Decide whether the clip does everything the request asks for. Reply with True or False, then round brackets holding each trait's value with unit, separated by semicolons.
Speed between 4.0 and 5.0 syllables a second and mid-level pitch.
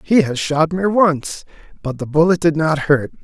True (4.5 syllables/s; 160 Hz)